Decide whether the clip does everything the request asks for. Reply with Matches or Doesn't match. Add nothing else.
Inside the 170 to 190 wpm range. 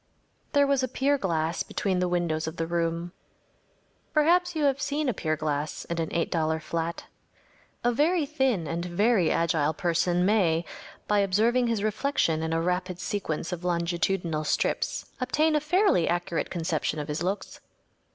Doesn't match